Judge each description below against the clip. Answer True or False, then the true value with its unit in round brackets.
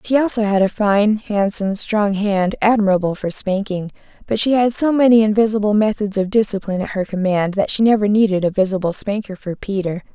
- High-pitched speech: True (205 Hz)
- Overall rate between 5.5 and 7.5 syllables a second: True (5.6 syllables/s)